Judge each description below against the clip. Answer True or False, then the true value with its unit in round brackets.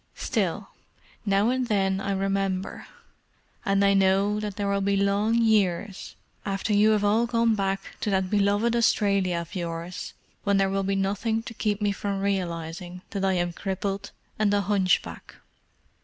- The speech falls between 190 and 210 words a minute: False (165 wpm)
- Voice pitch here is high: True (200 Hz)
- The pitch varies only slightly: True (1.4 semitones)